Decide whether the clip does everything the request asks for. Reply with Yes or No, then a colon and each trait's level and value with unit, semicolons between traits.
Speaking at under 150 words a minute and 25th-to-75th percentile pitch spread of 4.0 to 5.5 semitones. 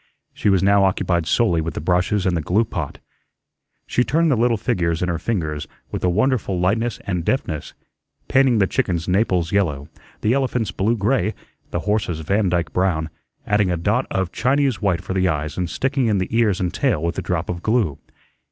No: average, 195 wpm; average, 4.5 semitones